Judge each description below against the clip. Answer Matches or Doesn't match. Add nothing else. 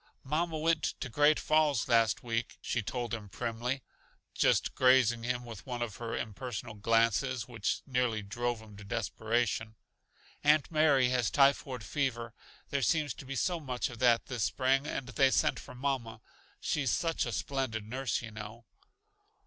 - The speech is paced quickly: Doesn't match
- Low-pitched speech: Matches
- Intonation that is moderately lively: Matches